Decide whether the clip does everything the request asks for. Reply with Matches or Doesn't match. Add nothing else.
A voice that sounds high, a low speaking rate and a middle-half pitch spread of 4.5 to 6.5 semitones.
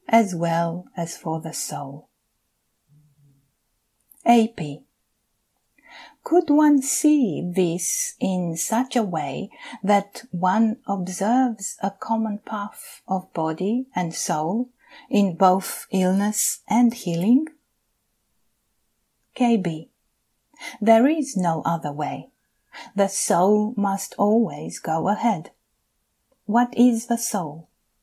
Matches